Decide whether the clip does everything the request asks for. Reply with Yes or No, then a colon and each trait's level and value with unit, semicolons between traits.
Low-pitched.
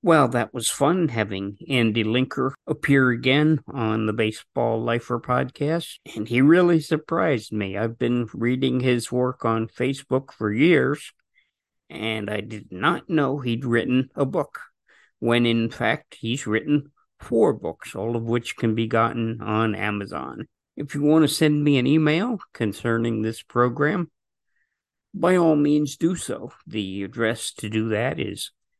Yes: low, 120 Hz